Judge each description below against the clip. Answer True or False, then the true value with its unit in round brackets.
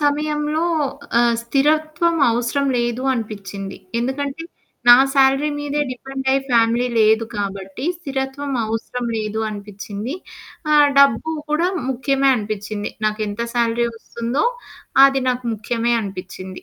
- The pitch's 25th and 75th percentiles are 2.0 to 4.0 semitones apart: False (4.5 semitones)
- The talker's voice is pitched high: True (240 Hz)